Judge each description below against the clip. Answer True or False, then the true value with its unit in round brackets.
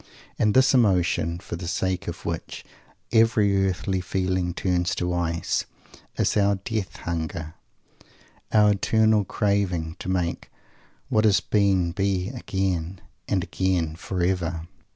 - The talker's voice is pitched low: True (95 Hz)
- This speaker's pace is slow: True (125 wpm)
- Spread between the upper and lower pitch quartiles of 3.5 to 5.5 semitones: False (2.6 semitones)